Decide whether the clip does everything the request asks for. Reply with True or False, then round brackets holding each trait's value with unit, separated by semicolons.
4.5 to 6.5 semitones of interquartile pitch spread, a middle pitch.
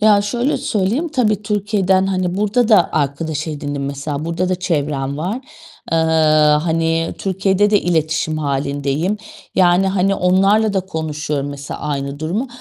True (5.0 semitones; 180 Hz)